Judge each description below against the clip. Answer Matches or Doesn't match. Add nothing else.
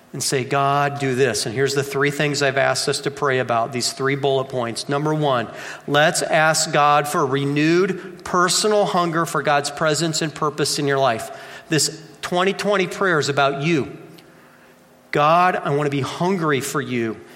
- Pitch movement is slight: Doesn't match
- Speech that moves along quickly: Doesn't match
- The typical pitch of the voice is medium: Matches